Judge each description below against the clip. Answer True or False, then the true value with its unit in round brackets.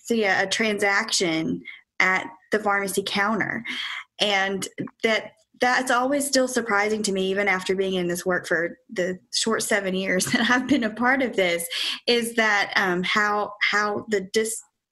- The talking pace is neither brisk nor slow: True (155 wpm)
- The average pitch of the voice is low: False (205 Hz)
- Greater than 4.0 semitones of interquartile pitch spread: False (3.2 semitones)